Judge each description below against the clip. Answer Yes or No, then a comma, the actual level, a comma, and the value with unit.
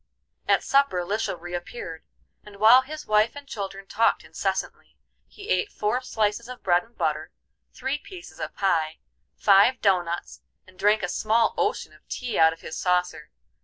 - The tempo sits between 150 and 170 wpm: Yes, average, 165 wpm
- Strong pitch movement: Yes, wide, 5.8 semitones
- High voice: Yes, high, 210 Hz